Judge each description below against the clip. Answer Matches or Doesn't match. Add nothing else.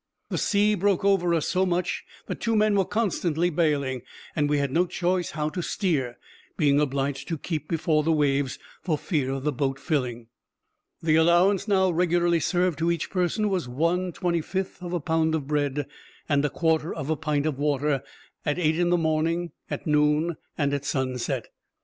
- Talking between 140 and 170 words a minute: Doesn't match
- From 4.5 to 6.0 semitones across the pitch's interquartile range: Doesn't match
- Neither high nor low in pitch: Matches